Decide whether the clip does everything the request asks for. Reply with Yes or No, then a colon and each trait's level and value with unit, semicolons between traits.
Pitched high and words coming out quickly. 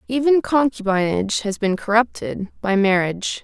No: high, 215 Hz; slow, 105 wpm